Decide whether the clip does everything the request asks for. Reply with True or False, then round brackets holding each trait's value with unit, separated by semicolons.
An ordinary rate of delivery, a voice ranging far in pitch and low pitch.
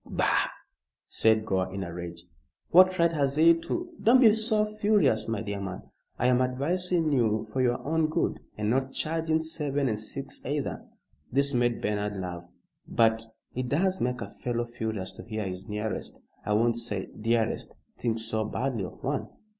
True (180 wpm; 6.6 semitones; 120 Hz)